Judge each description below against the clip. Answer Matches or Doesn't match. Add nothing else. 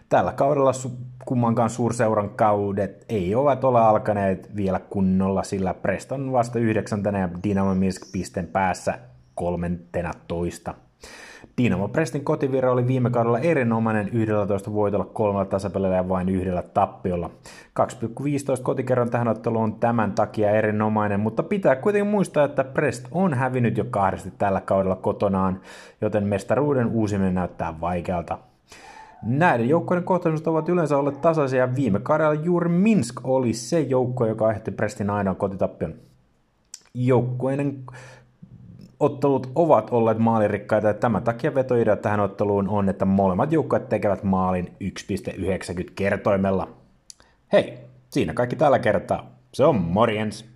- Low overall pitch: Matches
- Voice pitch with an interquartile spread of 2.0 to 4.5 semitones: Doesn't match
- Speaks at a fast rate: Doesn't match